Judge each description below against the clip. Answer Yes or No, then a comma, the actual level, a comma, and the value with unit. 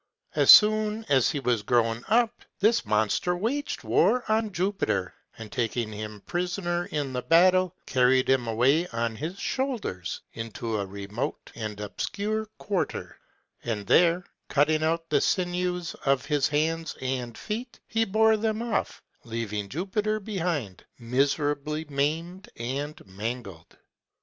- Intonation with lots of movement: Yes, wide, 8.5 semitones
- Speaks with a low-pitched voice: No, medium, 150 Hz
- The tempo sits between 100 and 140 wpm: Yes, slow, 135 wpm